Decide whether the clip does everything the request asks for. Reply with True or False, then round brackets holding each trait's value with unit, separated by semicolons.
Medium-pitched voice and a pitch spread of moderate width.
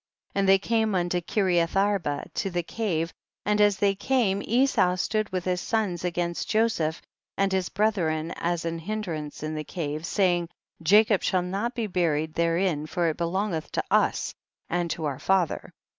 True (180 Hz; 3.4 semitones)